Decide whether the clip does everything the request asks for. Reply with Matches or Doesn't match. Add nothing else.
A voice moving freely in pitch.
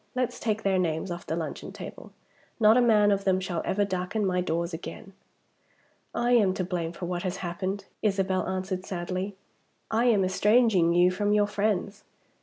Doesn't match